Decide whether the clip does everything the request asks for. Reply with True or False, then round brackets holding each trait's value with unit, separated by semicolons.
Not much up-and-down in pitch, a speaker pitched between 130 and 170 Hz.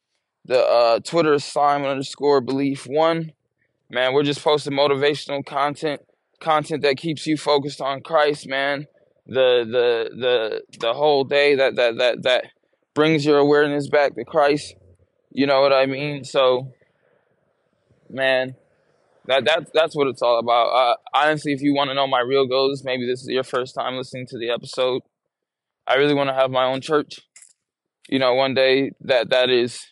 True (2.3 semitones; 140 Hz)